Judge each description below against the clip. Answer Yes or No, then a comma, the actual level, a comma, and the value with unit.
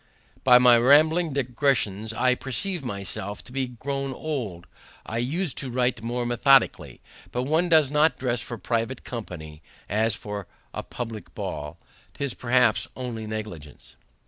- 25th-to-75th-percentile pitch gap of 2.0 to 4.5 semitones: Yes, average, 3.9 semitones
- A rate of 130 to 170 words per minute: Yes, average, 145 wpm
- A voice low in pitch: Yes, low, 125 Hz